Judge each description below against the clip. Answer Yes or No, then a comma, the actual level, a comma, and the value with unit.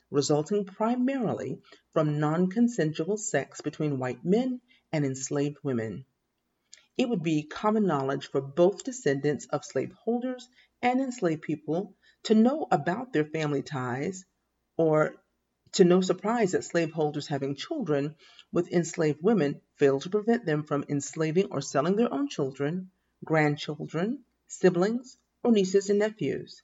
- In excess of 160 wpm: No, slow, 135 wpm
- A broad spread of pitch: Yes, wide, 6.3 semitones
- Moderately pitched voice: Yes, medium, 170 Hz